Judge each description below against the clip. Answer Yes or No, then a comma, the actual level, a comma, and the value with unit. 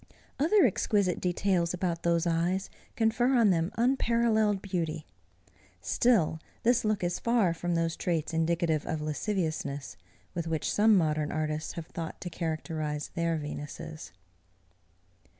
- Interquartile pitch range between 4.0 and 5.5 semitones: Yes, average, 4.5 semitones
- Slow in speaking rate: Yes, slow, 130 wpm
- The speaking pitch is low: No, medium, 170 Hz